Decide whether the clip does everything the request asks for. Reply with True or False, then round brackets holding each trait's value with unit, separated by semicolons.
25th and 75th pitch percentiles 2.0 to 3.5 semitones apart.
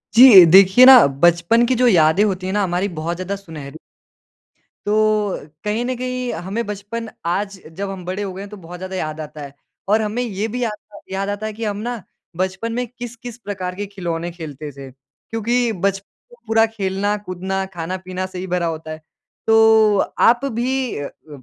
False (4.0 semitones)